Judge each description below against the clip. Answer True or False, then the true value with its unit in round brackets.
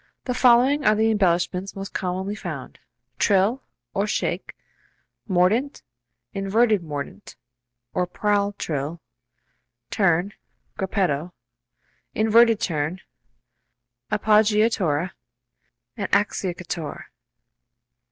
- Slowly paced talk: True (80 wpm)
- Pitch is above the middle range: True (195 Hz)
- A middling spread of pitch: True (3.5 semitones)